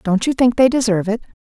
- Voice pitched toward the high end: Yes, high, 225 Hz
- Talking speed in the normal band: No, fast, 255 wpm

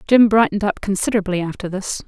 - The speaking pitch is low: No, high, 200 Hz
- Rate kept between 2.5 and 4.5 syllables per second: No, 6.7 syllables/s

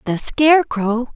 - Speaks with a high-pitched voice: Yes, very high, 250 Hz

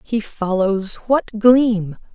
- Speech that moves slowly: Yes, slow, 110 wpm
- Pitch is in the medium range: No, high, 215 Hz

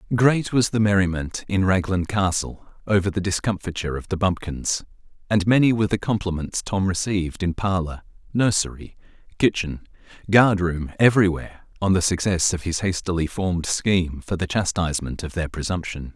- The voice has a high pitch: No, very low, 95 Hz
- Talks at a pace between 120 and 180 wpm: Yes, average, 150 wpm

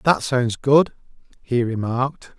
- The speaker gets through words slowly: Yes, slow, 125 wpm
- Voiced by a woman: No, male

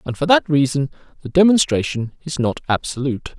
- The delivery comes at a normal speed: Yes, average, 160 wpm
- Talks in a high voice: No, medium, 145 Hz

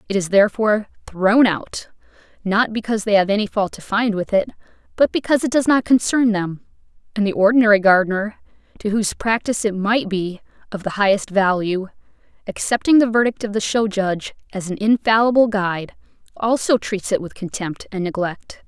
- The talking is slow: No, average, 175 wpm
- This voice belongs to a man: No, female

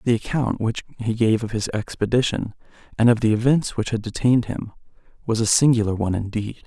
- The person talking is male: Yes, male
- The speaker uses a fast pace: No, average, 190 wpm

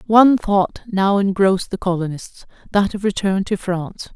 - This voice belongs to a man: No, female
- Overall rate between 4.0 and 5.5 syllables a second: Yes, 5.0 syllables/s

